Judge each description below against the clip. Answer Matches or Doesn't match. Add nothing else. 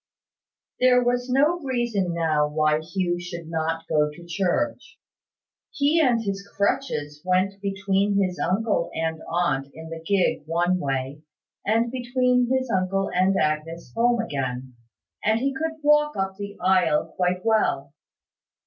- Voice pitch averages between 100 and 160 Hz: Doesn't match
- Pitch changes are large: Matches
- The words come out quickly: Doesn't match